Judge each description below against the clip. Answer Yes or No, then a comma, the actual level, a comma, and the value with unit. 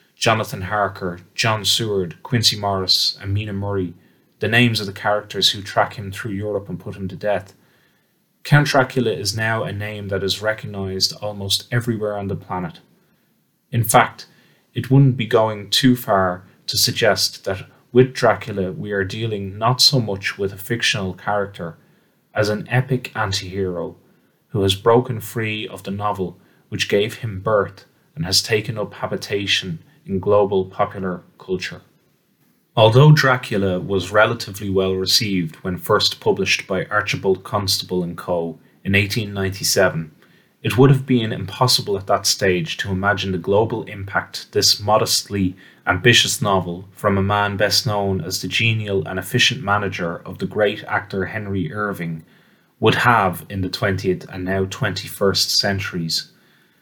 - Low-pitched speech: Yes, low, 100 Hz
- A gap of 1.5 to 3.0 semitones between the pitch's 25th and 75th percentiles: No, average, 3.4 semitones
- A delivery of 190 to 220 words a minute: No, average, 150 wpm